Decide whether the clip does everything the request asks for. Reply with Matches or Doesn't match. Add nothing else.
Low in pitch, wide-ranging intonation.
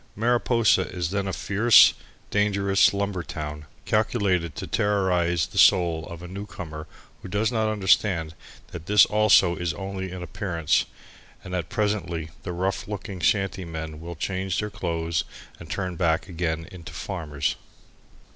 Doesn't match